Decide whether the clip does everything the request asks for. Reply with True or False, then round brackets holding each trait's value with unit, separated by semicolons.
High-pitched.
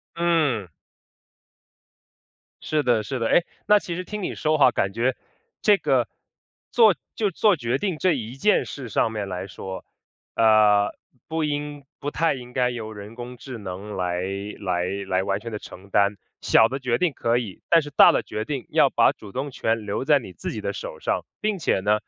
False (120 Hz)